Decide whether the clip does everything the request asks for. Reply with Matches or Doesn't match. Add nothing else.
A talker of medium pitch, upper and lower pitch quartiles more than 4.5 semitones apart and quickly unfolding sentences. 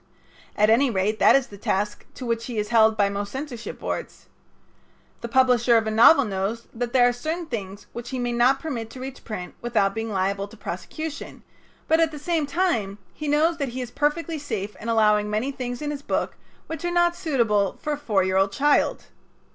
Doesn't match